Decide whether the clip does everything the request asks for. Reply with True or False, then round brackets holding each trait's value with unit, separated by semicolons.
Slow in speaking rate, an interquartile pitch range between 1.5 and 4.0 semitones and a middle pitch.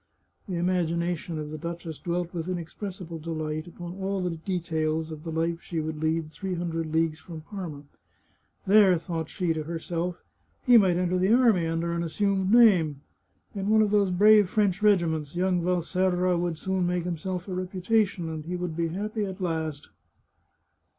False (175 wpm; 2.5 semitones; 175 Hz)